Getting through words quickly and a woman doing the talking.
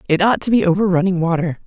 Yes: fast, 250 wpm; female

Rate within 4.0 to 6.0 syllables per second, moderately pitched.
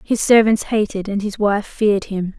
No: 4.8 syllables/s; high, 205 Hz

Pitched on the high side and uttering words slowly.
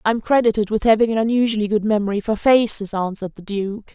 No: high, 215 Hz; average, 200 wpm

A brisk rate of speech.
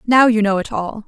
Yes: fast, 280 wpm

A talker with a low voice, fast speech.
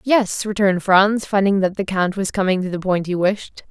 No: high, 195 Hz; fast, 225 wpm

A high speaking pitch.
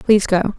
Yes: high, 200 Hz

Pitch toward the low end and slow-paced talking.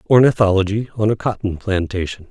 Yes: low, 100 Hz; slow, 130 wpm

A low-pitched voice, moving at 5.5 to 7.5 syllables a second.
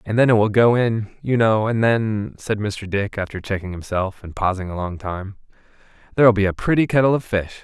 No: low, 105 Hz; 5.3 syllables/s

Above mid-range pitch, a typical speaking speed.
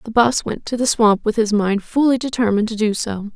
No: high, 220 Hz; fast, 250 wpm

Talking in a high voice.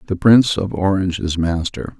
No: very low, 95 Hz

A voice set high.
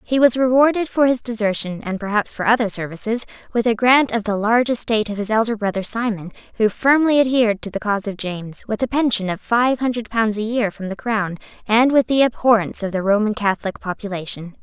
Yes: high, 220 Hz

